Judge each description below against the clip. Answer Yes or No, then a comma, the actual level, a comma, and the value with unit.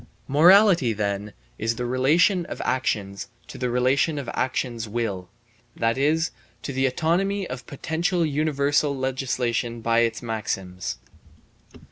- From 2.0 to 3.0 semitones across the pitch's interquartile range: No, average, 4.9 semitones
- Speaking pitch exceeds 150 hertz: No, low, 130 Hz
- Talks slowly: Yes, slow, 125 wpm